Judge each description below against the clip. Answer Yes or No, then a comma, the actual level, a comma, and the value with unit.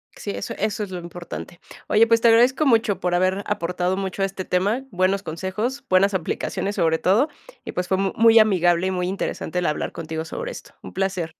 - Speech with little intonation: No, average, 3.3 semitones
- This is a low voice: No, high, 190 Hz